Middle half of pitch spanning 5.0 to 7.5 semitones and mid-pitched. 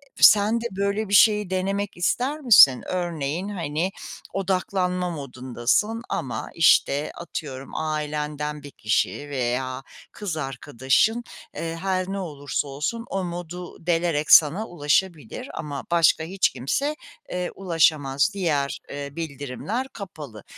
Yes: average, 5.3 semitones; medium, 165 Hz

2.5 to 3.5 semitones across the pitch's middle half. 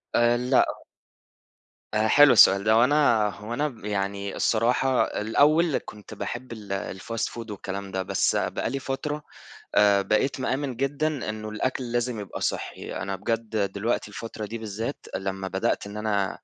No: average, 4.0 semitones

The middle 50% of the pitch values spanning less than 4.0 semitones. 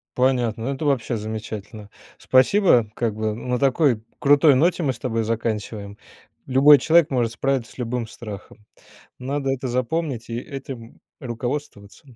Yes: average, 3.5 semitones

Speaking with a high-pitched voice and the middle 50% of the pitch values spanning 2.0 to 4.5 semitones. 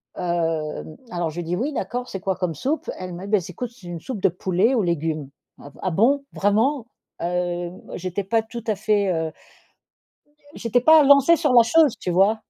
No: high, 195 Hz; wide, 5.6 semitones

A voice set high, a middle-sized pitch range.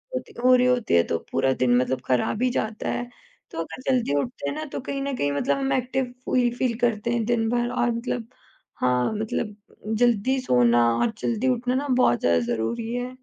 No: high, 235 Hz; wide, 7.6 semitones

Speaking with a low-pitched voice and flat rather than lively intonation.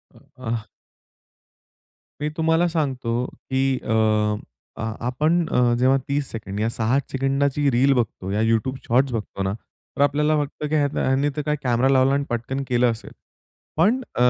No: low, 130 Hz; average, 3.4 semitones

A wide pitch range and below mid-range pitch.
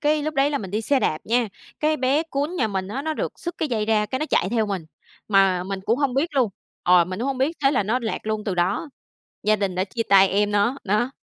No: wide, 5.9 semitones; high, 225 Hz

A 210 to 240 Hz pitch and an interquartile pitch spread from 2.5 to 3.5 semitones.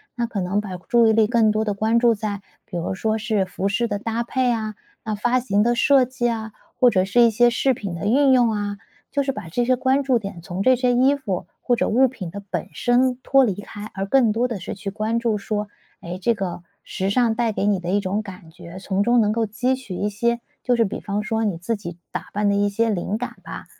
Yes: high, 215 Hz; average, 3.2 semitones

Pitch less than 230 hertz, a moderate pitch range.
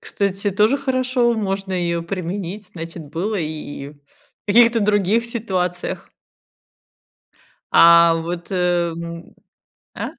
Yes: medium, 185 Hz; average, 3.9 semitones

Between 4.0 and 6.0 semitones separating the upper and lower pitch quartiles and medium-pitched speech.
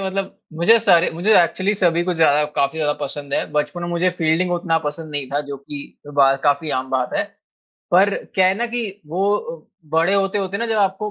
Yes: average, 4.5 semitones; medium, 170 Hz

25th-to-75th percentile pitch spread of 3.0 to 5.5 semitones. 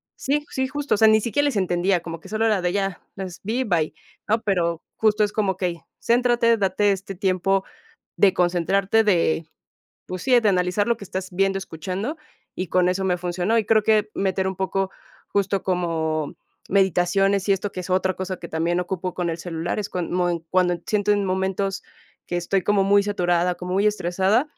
No: narrow, 2.6 semitones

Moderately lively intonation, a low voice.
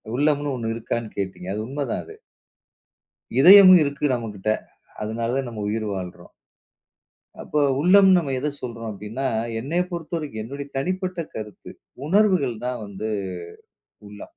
No: wide, 5.7 semitones; low, 130 Hz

